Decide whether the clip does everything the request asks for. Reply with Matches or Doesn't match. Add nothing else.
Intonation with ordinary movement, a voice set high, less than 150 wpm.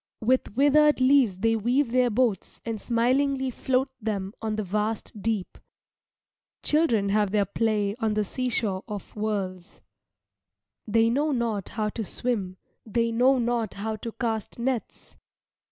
Matches